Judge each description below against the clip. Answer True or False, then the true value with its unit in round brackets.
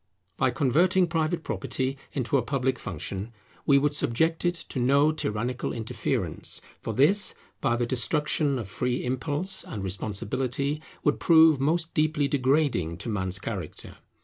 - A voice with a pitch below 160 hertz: True (135 Hz)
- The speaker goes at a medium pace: True (145 wpm)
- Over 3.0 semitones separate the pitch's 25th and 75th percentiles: True (4.8 semitones)